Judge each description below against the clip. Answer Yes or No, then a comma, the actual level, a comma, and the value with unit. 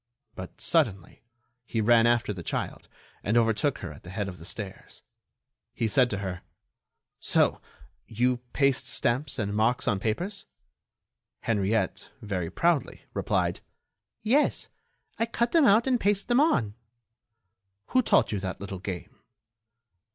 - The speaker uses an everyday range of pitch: No, wide, 7.2 semitones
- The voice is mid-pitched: No, low, 115 Hz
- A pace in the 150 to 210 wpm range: No, average, 140 wpm